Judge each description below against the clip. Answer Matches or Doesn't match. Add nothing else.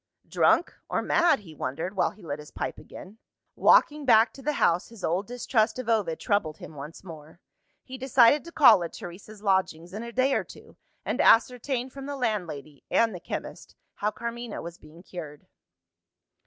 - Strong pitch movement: Matches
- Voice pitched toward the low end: Doesn't match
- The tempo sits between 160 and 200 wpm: Matches